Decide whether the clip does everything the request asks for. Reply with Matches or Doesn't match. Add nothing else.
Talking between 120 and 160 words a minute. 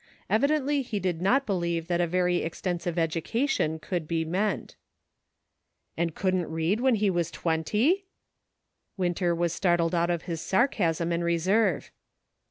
Matches